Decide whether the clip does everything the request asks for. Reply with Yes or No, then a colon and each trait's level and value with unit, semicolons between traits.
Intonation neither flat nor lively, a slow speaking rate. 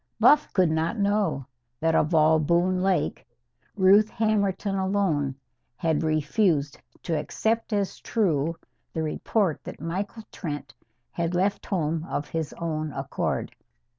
Yes: average, 4.3 semitones; slow, 130 wpm